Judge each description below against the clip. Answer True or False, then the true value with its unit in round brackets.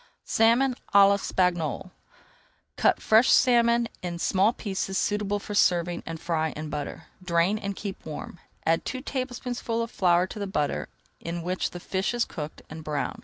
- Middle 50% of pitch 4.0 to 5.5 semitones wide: True (4.9 semitones)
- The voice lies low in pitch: False (190 Hz)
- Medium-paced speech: True (165 wpm)